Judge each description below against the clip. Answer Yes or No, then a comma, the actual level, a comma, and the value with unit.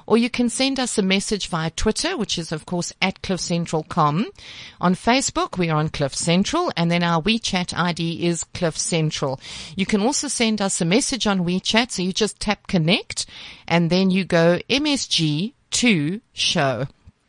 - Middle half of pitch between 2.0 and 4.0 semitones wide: No, average, 4.6 semitones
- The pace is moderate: Yes, average, 175 wpm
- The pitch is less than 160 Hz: No, medium, 185 Hz